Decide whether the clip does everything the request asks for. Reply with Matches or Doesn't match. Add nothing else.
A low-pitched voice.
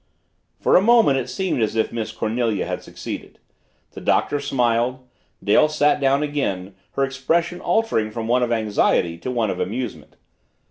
Matches